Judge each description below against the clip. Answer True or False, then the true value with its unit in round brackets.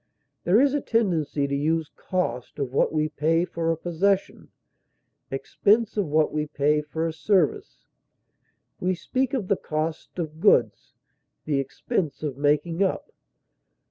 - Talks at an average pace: True (145 wpm)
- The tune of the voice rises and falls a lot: False (3.8 semitones)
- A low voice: False (160 Hz)